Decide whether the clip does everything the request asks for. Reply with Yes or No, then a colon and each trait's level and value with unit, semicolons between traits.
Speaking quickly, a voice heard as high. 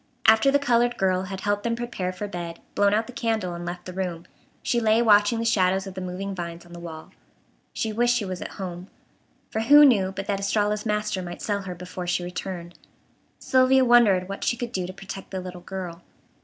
Yes: fast, 220 wpm; high, 195 Hz